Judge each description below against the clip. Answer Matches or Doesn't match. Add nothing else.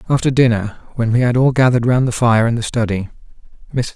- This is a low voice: Matches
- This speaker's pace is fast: Doesn't match